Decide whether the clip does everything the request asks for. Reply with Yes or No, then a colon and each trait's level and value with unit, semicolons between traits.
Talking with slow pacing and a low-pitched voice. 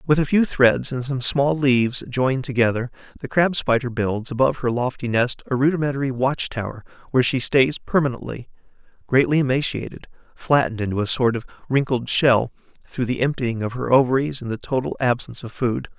No: average, 175 wpm; low, 130 Hz